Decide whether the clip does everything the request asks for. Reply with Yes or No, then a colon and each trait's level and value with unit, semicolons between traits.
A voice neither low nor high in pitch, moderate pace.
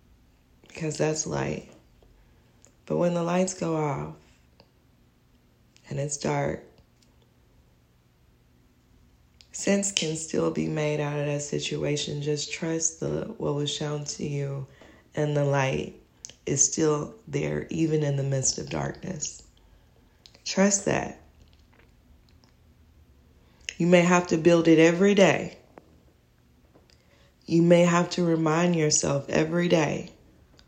No: medium, 145 Hz; slow, 115 wpm